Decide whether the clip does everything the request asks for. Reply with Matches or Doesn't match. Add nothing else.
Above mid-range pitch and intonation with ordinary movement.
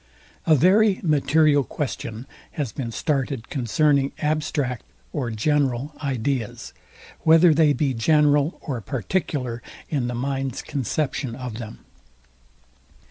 Doesn't match